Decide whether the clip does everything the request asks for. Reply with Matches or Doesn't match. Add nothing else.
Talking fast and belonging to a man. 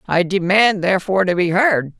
Doesn't match